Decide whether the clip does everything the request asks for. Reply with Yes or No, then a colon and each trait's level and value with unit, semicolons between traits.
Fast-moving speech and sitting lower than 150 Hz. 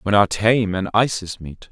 Yes: fast, 210 wpm; low, 100 Hz